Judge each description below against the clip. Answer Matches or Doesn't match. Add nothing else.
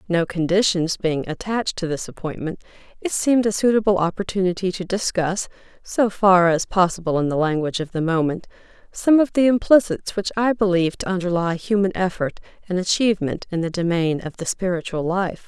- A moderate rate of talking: Matches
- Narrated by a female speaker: Matches